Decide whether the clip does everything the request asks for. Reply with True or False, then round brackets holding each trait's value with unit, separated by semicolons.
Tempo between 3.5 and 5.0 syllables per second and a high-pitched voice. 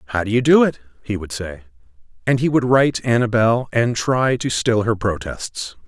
False (4.7 syllables/s; 115 Hz)